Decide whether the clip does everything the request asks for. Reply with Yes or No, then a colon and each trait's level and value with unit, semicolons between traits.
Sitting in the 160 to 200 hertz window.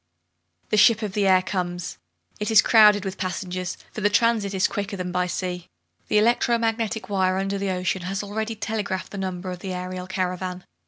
Yes: high, 190 Hz